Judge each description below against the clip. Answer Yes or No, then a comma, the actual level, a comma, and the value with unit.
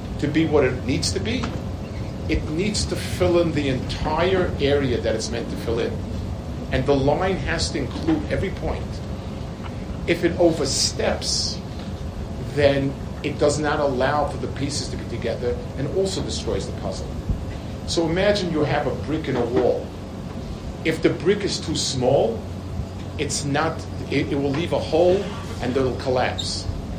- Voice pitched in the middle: No, low, 125 Hz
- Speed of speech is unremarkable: Yes, average, 165 wpm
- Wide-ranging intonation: Yes, wide, 7.6 semitones